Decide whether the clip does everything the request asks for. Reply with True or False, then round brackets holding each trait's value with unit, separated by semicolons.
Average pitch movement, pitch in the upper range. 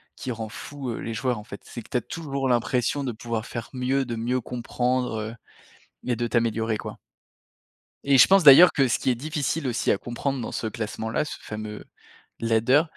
False (3.0 semitones; 120 Hz)